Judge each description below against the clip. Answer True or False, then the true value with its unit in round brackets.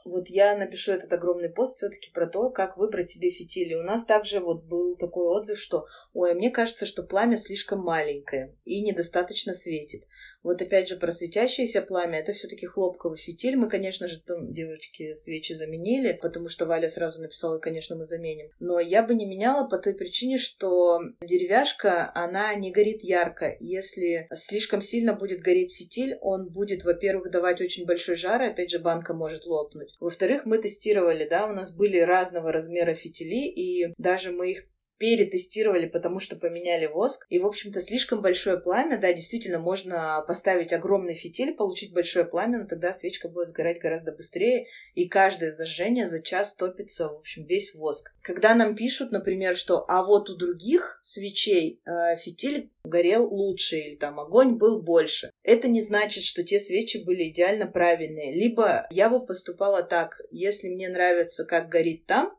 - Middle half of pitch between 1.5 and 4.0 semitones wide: True (3.7 semitones)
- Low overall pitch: False (185 Hz)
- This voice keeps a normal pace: False (175 wpm)